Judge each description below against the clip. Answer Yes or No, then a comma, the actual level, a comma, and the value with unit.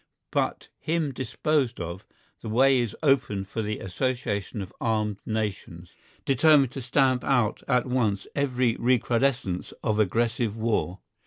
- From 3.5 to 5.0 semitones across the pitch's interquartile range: Yes, average, 3.8 semitones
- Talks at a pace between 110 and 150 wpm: Yes, slow, 135 wpm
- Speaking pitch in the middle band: No, low, 120 Hz